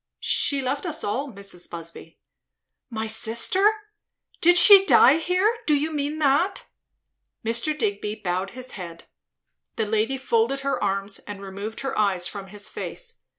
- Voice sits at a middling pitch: No, high, 235 Hz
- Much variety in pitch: Yes, wide, 7.3 semitones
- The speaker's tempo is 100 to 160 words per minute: Yes, average, 150 wpm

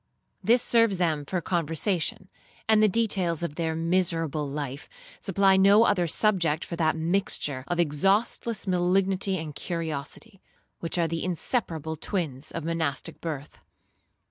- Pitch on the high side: No, medium, 170 Hz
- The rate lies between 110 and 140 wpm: Yes, slow, 135 wpm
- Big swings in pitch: No, average, 3.5 semitones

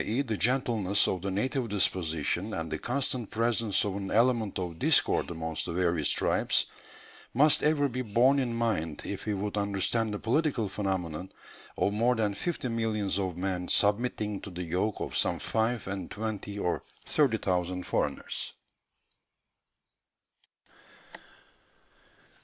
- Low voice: Yes, low, 105 Hz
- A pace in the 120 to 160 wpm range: Yes, average, 140 wpm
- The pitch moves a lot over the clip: No, average, 4.1 semitones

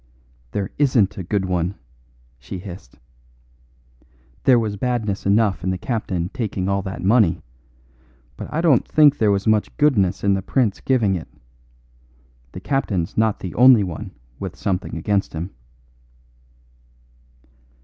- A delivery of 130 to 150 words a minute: Yes, average, 140 wpm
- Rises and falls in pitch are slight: No, average, 3.8 semitones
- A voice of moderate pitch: No, low, 100 Hz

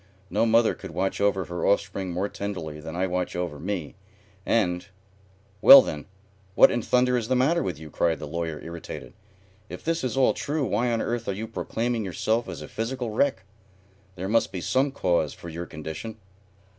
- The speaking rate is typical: Yes, average, 195 wpm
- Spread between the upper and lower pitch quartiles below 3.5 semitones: No, average, 5.2 semitones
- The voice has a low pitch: Yes, low, 100 Hz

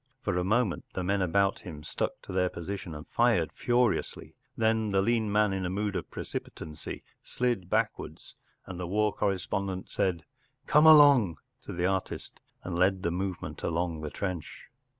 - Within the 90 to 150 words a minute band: No, average, 170 wpm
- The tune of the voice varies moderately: Yes, average, 3.2 semitones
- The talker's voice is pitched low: Yes, very low, 95 Hz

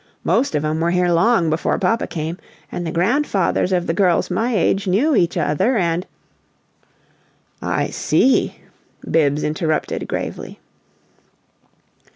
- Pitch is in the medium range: Yes, medium, 175 Hz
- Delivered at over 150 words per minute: No, average, 140 wpm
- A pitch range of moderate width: Yes, average, 3.8 semitones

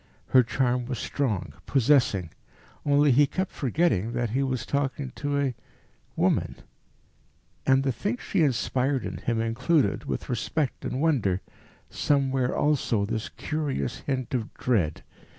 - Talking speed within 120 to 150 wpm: Yes, slow, 135 wpm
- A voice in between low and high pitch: No, low, 130 Hz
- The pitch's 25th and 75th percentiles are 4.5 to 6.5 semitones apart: No, average, 3.3 semitones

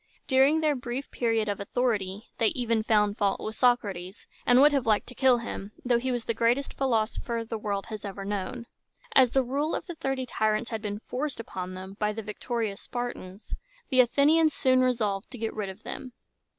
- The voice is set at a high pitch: Yes, high, 230 Hz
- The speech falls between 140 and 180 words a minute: No, average, 200 wpm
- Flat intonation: No, average, 3.6 semitones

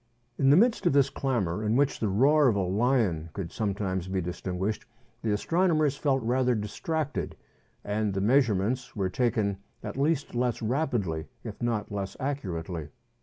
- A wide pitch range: Yes, wide, 5.7 semitones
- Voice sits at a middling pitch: No, low, 110 Hz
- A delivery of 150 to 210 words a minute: Yes, average, 160 wpm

